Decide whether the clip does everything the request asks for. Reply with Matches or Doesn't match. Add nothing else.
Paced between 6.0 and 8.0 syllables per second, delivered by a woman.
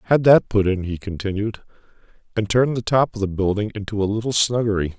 Doesn't match